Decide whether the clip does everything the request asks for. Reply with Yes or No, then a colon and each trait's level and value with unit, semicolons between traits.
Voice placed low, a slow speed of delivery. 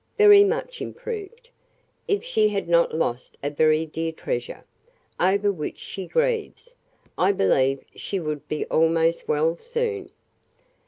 No: high, 190 Hz; slow, 130 wpm